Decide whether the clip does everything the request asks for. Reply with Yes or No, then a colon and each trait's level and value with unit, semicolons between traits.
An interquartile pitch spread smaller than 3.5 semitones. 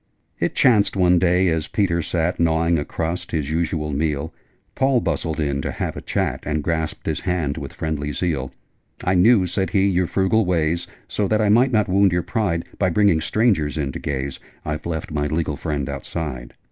No: average, 3.8 semitones